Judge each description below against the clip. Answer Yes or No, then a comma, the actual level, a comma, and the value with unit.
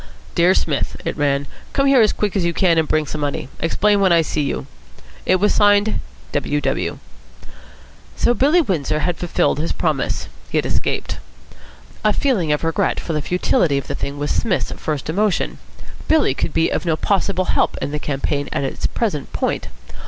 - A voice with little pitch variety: No, wide, 5.6 semitones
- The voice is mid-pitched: Yes, medium, 170 Hz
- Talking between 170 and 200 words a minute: Yes, average, 190 wpm